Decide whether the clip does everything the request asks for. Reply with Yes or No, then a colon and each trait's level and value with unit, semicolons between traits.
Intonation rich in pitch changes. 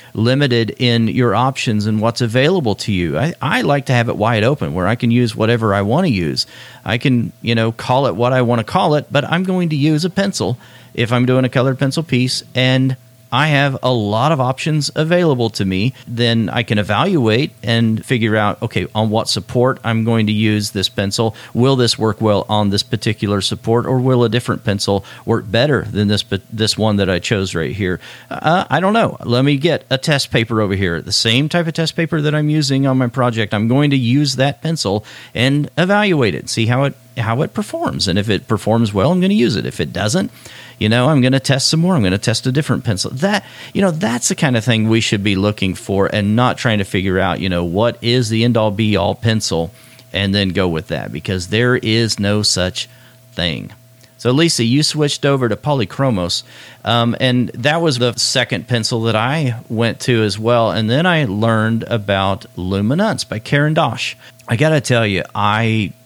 No: average, 3.8 semitones